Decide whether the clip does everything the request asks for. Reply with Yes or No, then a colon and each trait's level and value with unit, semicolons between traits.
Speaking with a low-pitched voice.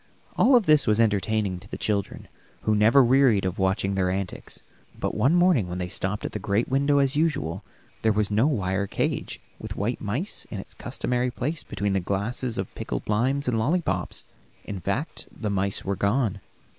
Yes: low, 105 Hz